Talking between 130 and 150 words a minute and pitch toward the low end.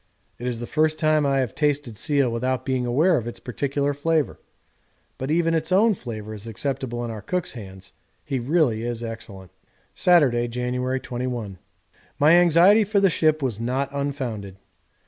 No: average, 165 wpm; low, 130 Hz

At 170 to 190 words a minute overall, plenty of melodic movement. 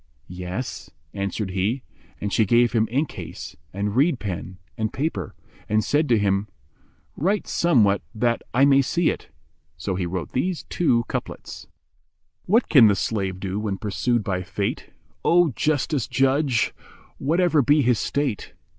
No: average, 155 wpm; wide, 6.3 semitones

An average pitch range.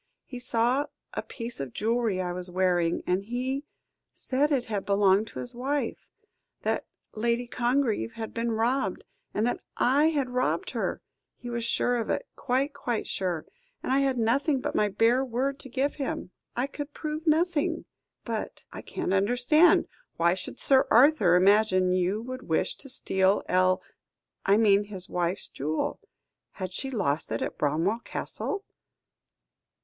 No: wide, 5.7 semitones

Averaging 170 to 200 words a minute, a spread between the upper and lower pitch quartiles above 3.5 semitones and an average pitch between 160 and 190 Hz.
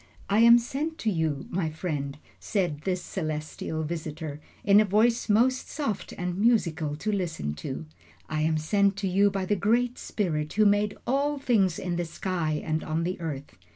Yes: average, 180 wpm; average, 5.2 semitones; medium, 185 Hz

